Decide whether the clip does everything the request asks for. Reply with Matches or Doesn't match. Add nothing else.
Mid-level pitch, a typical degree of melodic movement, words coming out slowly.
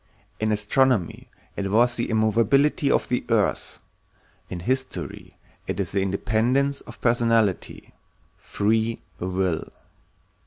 Doesn't match